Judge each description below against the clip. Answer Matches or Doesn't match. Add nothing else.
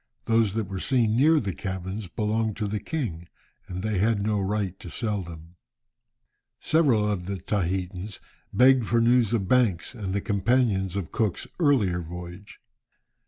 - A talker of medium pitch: Doesn't match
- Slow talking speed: Doesn't match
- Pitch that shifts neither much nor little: Matches